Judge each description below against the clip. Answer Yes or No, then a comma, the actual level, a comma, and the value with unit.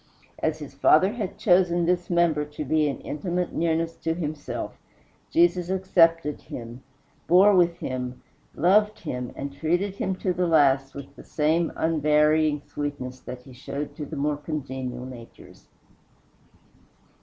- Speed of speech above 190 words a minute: No, average, 145 wpm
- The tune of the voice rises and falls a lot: No, average, 3.9 semitones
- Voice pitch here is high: No, medium, 155 Hz